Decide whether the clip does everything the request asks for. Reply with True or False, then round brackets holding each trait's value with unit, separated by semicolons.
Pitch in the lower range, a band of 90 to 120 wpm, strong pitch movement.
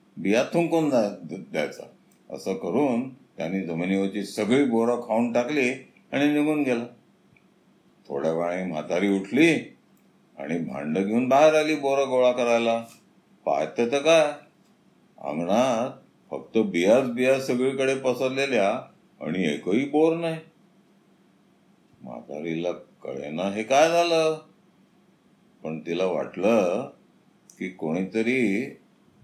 True (125 Hz; 100 wpm; 6.7 semitones)